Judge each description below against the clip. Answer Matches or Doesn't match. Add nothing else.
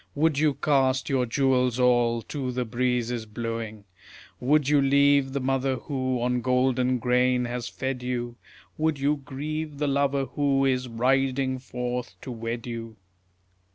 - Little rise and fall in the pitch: Matches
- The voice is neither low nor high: Doesn't match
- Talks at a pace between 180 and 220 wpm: Doesn't match